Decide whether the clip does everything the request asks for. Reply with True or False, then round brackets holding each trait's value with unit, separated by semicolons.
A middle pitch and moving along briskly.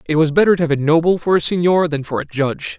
True (160 Hz; 300 wpm)